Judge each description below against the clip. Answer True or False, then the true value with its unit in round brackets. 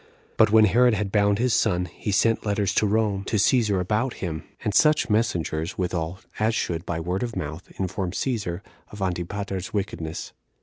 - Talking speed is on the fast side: False (175 wpm)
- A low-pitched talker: True (100 Hz)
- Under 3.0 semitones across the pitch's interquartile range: False (3.6 semitones)